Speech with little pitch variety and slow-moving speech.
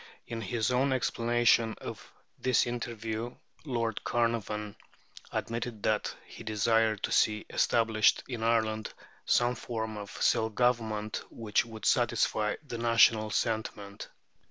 Yes: narrow, 1.5 semitones; slow, 120 wpm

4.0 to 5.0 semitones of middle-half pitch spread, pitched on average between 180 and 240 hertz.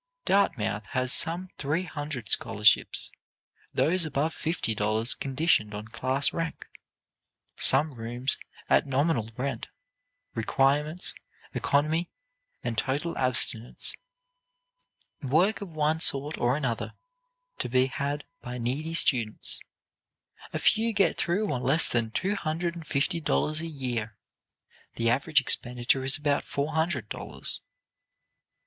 No: average, 4.7 semitones; medium, 140 Hz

